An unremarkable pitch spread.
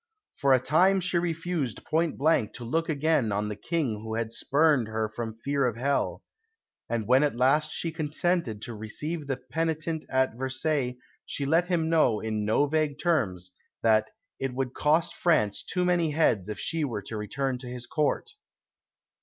No: wide, 5.9 semitones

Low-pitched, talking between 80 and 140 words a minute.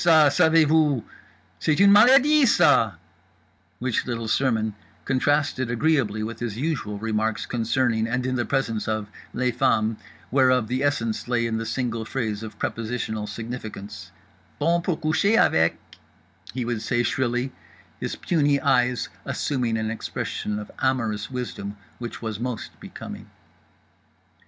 Yes: low, 120 Hz; slow, 135 wpm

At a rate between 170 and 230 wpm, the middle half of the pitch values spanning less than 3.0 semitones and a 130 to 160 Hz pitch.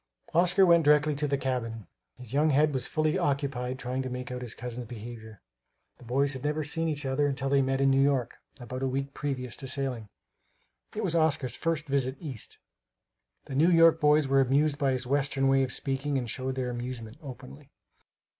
Yes: average, 200 wpm; narrow, 2.5 semitones; low, 135 Hz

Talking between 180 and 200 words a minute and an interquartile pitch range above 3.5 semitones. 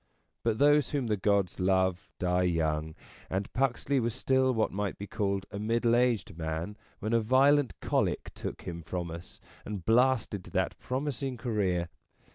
No: average, 165 wpm; wide, 5.5 semitones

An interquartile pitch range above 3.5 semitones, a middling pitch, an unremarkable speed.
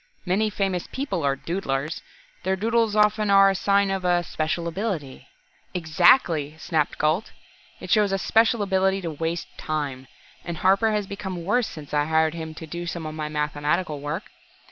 Yes: average, 4.2 semitones; medium, 175 Hz; average, 170 wpm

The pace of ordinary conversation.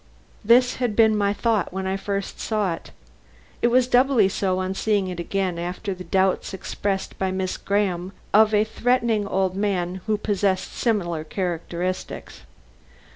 Yes: average, 155 wpm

